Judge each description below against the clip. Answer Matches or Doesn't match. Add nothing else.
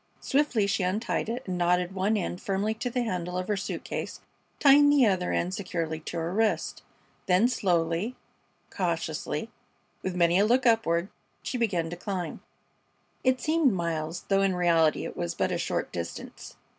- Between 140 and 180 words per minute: Matches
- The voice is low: Doesn't match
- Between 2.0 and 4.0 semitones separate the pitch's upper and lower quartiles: Doesn't match